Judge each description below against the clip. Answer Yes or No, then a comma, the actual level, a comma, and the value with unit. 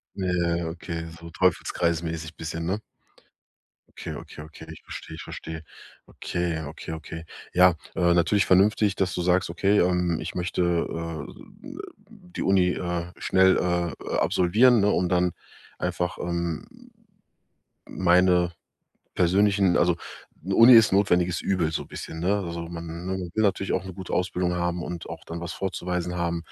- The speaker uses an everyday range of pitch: No, narrow, 1.9 semitones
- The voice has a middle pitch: No, very low, 90 Hz